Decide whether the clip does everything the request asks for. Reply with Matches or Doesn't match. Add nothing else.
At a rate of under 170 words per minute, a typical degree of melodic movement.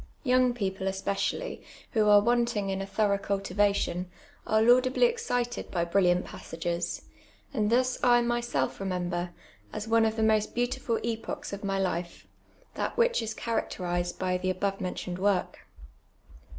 Matches